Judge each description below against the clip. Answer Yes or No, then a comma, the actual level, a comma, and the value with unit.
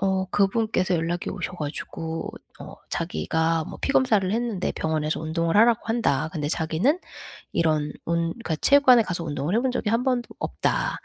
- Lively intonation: Yes, wide, 6.3 semitones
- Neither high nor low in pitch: Yes, medium, 180 Hz